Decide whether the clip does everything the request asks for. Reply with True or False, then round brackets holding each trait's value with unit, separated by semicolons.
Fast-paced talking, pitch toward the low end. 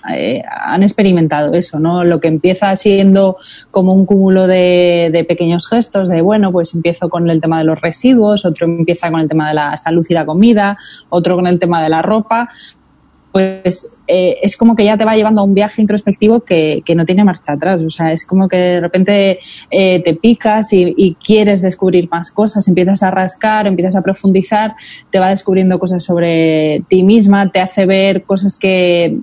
False (200 wpm; 185 Hz)